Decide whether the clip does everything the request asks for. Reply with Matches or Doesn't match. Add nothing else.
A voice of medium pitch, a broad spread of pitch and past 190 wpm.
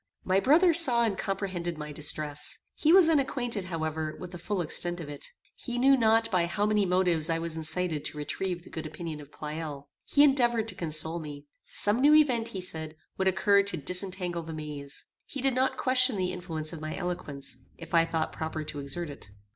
Matches